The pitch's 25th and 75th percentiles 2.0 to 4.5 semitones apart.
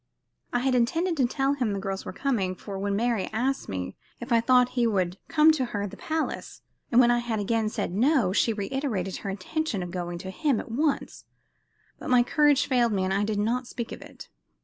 No: average, 4.9 semitones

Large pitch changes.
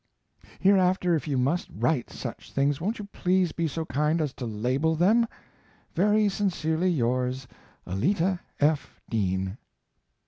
Yes: wide, 6.2 semitones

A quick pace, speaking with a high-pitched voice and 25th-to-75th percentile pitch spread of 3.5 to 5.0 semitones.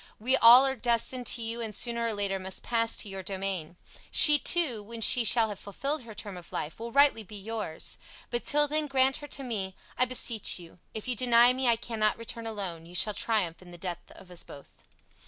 Yes: fast, 225 wpm; high, 225 Hz; average, 4.2 semitones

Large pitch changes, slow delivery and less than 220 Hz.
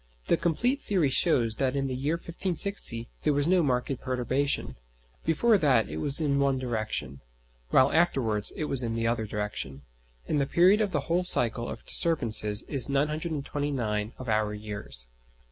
No: wide, 5.9 semitones; average, 165 wpm; low, 135 Hz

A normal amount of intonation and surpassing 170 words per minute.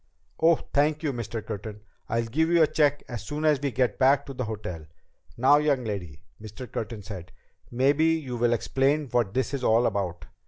Yes: average, 5.0 semitones; average, 195 wpm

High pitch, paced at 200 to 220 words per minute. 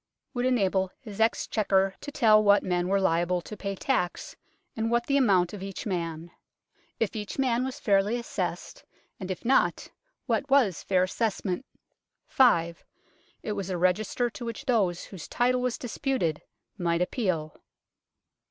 No: high, 200 Hz; average, 150 wpm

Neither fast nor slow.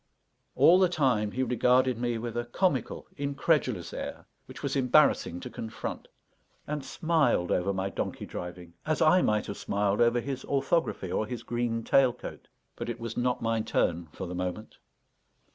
Yes: average, 170 wpm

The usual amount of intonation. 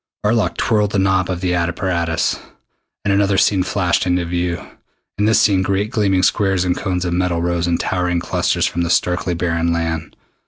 No: narrow, 2.0 semitones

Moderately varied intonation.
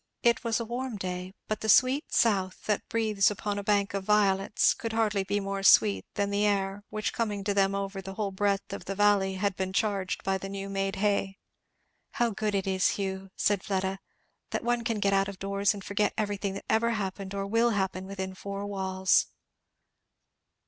No: narrow, 1.4 semitones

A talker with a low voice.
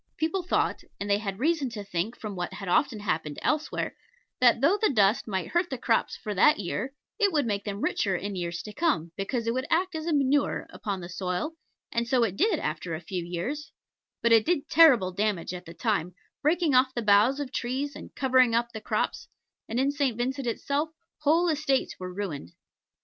No: high, 235 Hz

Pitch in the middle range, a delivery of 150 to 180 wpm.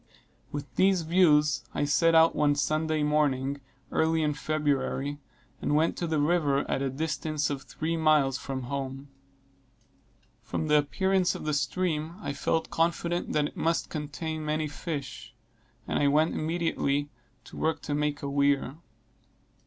Yes: medium, 150 Hz; average, 155 wpm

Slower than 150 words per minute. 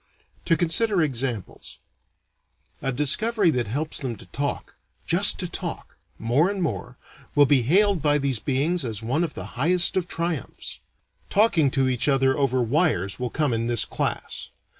No: average, 160 wpm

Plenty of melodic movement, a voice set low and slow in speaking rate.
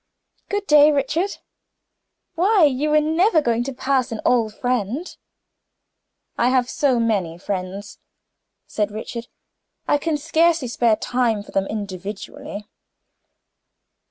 No: wide, 6.0 semitones; very high, 250 Hz; slow, 120 wpm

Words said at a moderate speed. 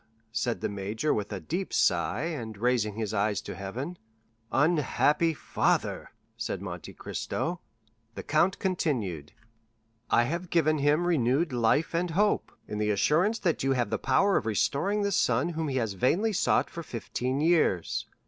Yes: average, 160 wpm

